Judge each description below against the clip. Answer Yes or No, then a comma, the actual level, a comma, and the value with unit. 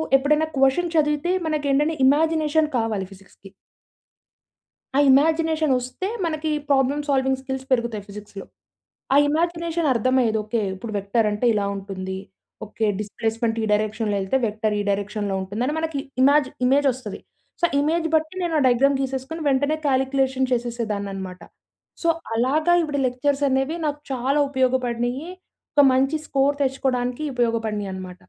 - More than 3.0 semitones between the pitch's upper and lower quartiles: Yes, average, 4.9 semitones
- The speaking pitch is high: Yes, very high, 260 Hz